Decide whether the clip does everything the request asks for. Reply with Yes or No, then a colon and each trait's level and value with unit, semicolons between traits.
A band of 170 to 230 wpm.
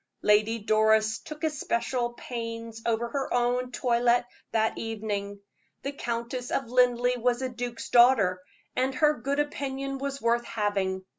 No: average, 140 wpm